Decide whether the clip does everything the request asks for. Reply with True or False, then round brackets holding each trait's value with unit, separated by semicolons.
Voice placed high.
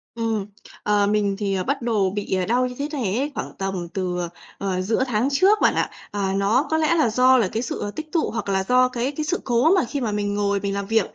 True (220 Hz)